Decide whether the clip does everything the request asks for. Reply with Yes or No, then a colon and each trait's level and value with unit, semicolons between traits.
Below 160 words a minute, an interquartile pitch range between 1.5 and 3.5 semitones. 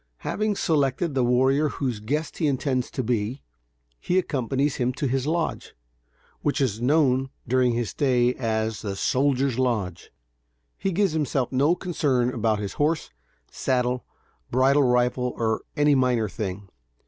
Yes: average, 145 wpm; average, 3.1 semitones